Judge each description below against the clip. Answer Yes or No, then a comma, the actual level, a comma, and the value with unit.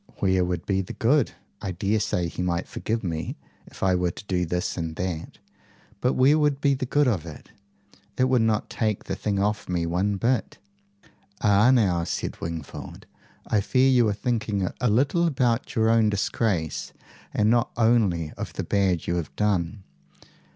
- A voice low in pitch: Yes, low, 105 Hz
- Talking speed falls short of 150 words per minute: No, average, 180 wpm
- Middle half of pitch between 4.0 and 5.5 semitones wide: Yes, average, 4.8 semitones